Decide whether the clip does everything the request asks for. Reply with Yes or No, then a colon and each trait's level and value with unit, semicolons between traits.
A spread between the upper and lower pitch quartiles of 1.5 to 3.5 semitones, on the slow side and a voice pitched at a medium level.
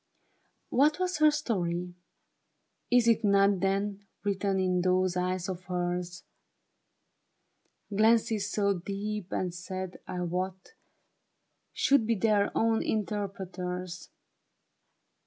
No: average, 2.8 semitones; slow, 100 wpm; high, 195 Hz